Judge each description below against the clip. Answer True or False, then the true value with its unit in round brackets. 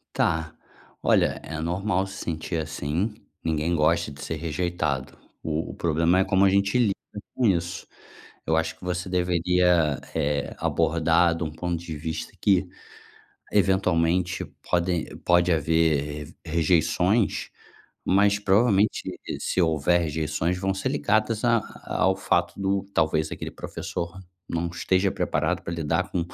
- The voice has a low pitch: True (85 Hz)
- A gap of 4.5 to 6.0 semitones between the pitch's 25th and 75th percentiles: False (2.8 semitones)